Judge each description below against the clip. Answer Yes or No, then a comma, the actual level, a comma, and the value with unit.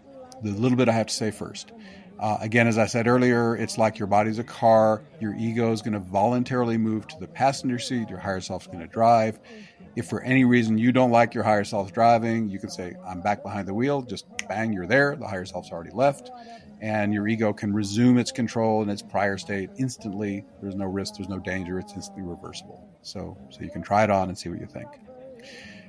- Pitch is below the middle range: Yes, low, 110 Hz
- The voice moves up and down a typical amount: Yes, average, 3.5 semitones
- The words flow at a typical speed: No, fast, 230 wpm